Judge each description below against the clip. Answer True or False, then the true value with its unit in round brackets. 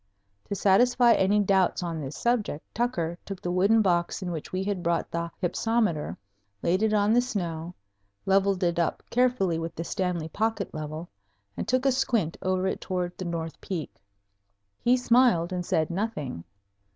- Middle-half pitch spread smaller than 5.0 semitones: True (4.5 semitones)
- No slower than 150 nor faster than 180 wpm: True (170 wpm)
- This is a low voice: False (185 Hz)